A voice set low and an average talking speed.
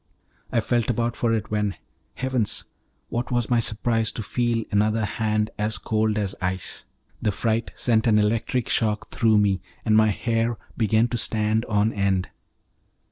Yes: low, 110 Hz; average, 160 wpm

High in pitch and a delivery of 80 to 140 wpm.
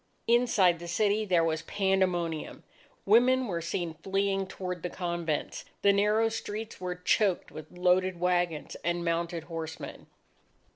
No: medium, 180 Hz; slow, 135 wpm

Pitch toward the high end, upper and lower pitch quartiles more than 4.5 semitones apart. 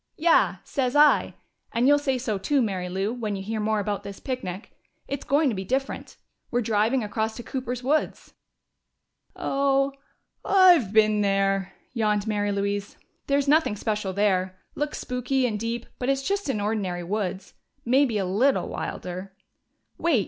Yes: high, 220 Hz; average, 5.0 semitones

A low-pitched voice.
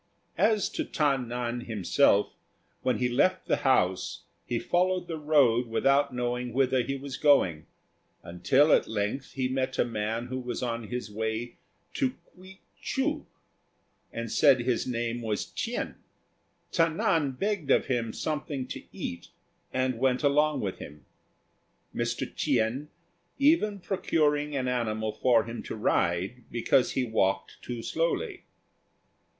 Yes: low, 125 Hz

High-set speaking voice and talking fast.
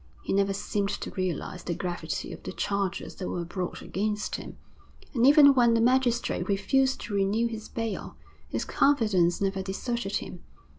No: high, 205 Hz; average, 165 wpm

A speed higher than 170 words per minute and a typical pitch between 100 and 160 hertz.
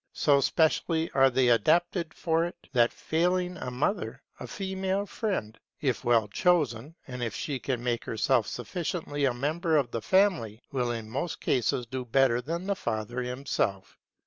No: average, 165 wpm; low, 135 Hz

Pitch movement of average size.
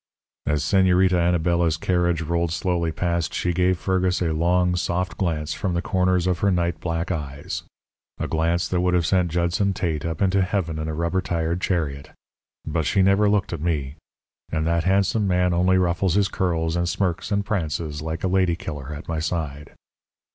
No: narrow, 2.2 semitones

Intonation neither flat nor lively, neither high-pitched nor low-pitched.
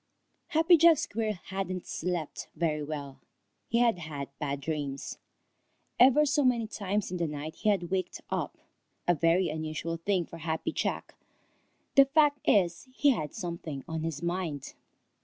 No: wide, 5.9 semitones; medium, 175 Hz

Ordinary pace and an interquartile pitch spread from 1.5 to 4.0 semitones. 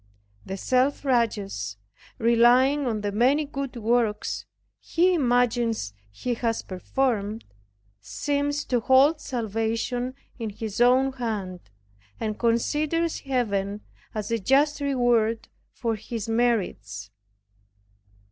No: slow, 105 wpm; average, 3.7 semitones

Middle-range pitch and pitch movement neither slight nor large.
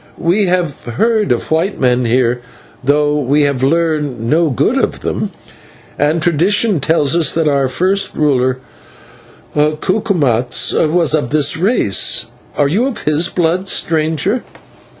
Yes: medium, 155 Hz; average, 4.2 semitones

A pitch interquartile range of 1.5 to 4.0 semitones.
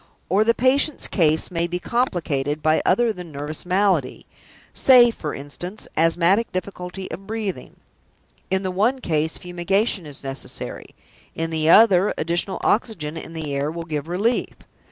No: average, 4.6 semitones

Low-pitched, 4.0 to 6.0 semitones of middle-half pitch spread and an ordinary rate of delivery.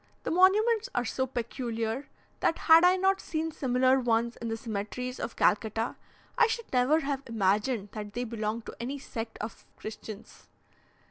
No: high, 245 Hz; wide, 5.5 semitones; average, 160 wpm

